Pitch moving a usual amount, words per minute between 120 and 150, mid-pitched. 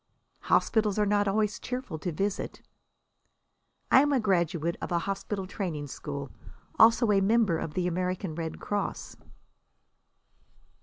No: average, 3.8 semitones; slow, 135 wpm; high, 195 Hz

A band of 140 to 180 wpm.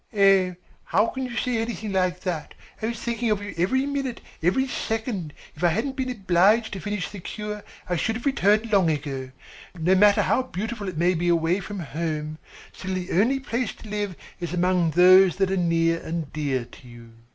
No: average, 200 wpm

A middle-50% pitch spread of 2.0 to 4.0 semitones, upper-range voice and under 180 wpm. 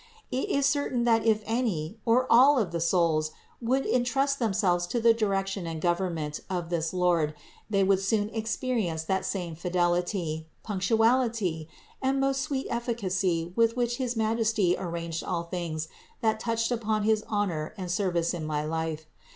No: average, 5.2 semitones; high, 195 Hz; average, 160 wpm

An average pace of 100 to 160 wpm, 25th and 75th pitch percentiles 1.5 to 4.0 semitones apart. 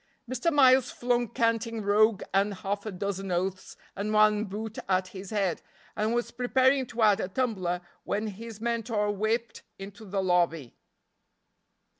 Yes: average, 150 wpm; average, 3.0 semitones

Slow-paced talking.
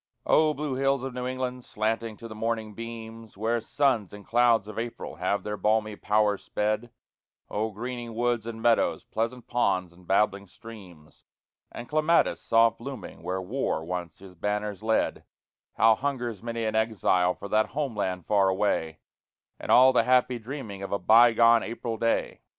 No: average, 165 wpm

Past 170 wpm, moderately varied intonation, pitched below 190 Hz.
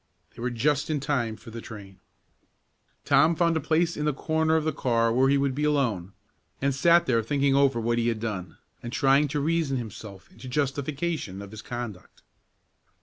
Yes: average, 195 wpm; average, 4.5 semitones; low, 135 Hz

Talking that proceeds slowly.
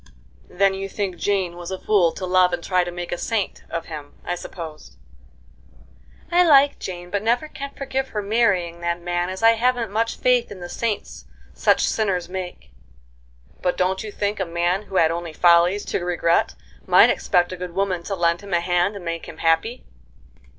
No: average, 195 wpm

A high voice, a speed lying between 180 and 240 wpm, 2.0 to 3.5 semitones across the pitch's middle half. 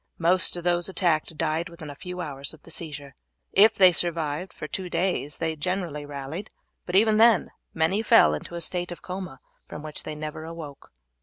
No: medium, 165 Hz; average, 190 wpm; average, 3.2 semitones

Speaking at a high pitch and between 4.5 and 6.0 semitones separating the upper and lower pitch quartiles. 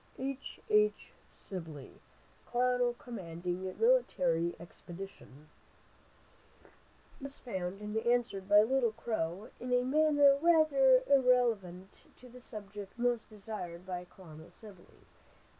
Yes: high, 220 Hz; wide, 5.6 semitones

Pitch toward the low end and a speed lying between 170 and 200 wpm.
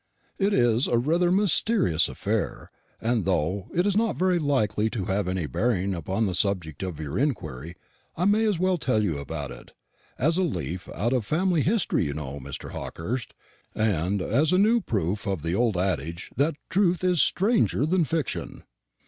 Yes: low, 110 Hz; average, 180 wpm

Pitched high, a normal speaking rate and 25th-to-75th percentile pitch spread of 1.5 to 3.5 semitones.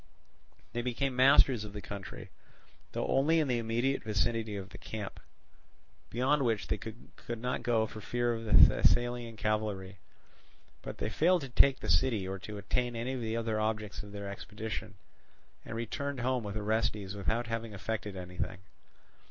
No: low, 110 Hz; average, 170 wpm; average, 2.8 semitones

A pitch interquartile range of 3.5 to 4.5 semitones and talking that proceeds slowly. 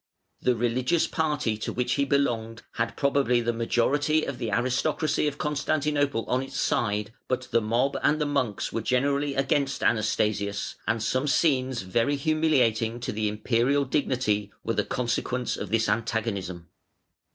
No: average, 3.8 semitones; average, 150 wpm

